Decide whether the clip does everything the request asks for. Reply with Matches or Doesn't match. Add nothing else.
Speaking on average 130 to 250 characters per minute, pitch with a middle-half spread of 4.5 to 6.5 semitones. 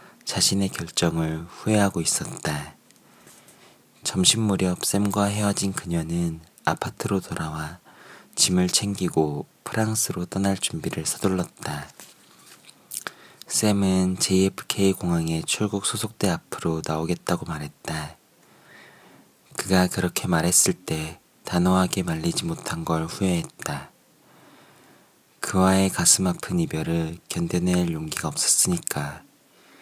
Doesn't match